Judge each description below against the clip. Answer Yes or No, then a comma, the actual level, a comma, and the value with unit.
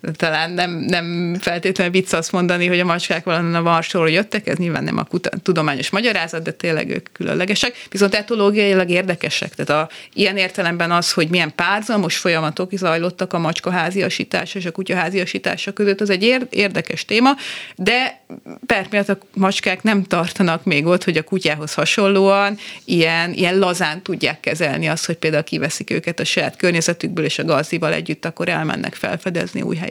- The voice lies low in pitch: No, medium, 180 Hz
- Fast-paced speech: Yes, fast, 165 wpm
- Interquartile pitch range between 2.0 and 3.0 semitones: Yes, average, 2.7 semitones